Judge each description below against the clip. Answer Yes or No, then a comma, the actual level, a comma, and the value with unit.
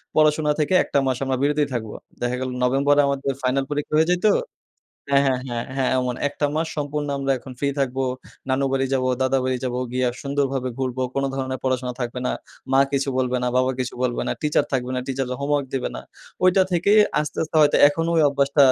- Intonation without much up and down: Yes, narrow, 2.1 semitones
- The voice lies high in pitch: No, low, 135 Hz